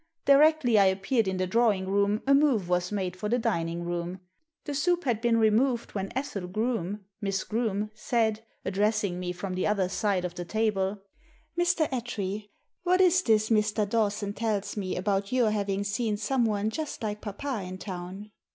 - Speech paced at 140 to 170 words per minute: No, average, 185 wpm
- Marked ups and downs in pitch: No, average, 3.5 semitones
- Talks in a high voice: Yes, high, 210 Hz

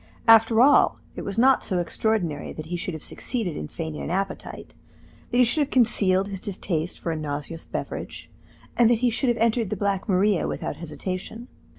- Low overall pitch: No, high, 195 Hz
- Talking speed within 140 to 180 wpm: No, average, 195 wpm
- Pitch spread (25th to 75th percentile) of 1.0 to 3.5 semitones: No, average, 5.1 semitones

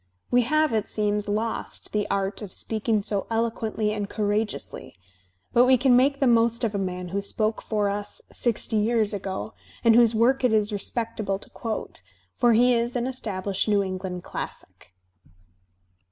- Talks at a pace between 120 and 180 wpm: Yes, average, 170 wpm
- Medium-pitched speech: No, high, 220 Hz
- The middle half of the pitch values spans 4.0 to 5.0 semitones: No, narrow, 2.5 semitones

